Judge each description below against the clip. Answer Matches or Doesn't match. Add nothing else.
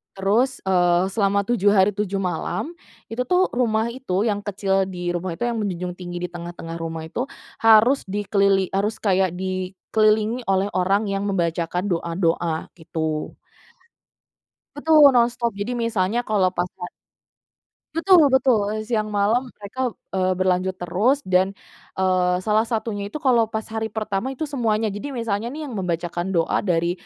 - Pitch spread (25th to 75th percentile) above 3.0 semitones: Matches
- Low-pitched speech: Doesn't match